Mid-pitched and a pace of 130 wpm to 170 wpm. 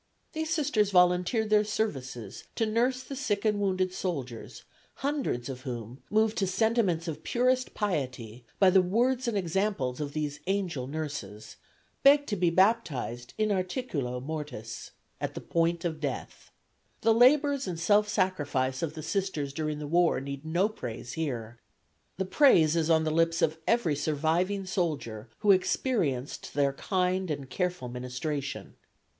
Yes: medium, 170 Hz; average, 155 wpm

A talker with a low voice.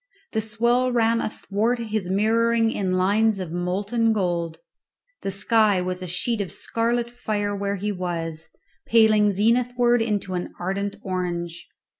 No: high, 205 Hz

